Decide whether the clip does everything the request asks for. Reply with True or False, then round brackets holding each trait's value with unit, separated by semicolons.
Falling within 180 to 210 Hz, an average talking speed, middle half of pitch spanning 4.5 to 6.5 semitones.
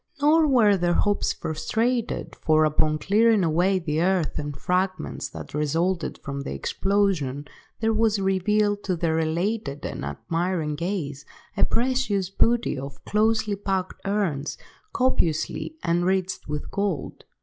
False (185 Hz; 130 wpm; 5.1 semitones)